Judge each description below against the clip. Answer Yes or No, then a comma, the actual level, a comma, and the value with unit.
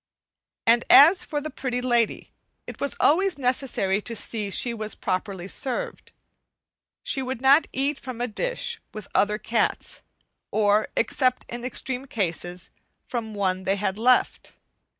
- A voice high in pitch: Yes, high, 240 Hz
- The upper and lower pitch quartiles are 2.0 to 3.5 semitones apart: No, average, 4.5 semitones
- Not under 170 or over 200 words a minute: No, average, 150 wpm